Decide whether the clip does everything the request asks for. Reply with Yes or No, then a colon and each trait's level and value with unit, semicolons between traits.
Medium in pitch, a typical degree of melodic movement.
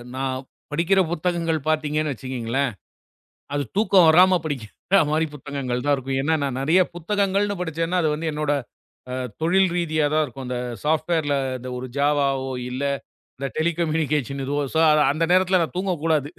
Yes: medium, 155 Hz; average, 3.7 semitones